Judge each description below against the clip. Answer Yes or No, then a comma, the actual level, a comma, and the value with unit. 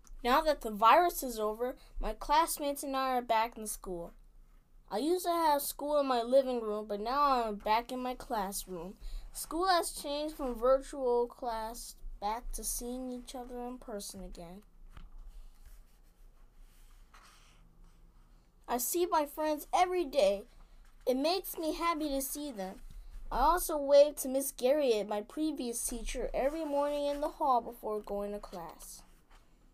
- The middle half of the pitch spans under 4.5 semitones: No, average, 5.1 semitones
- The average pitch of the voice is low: No, very high, 255 Hz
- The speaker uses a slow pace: No, average, 150 wpm